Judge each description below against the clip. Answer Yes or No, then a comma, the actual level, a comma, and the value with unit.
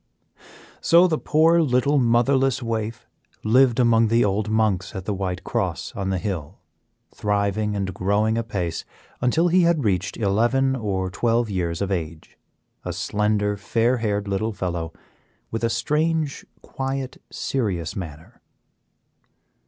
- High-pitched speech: No, low, 110 Hz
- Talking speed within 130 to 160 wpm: Yes, slow, 135 wpm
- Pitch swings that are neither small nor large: Yes, average, 4.6 semitones